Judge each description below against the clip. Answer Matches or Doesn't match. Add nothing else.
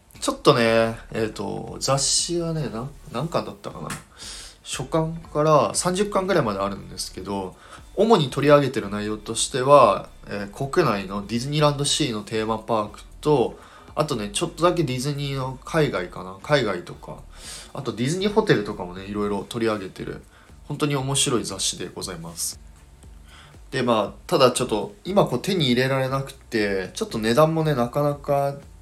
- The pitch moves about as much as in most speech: Doesn't match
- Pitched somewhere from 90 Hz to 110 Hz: Doesn't match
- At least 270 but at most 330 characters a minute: Doesn't match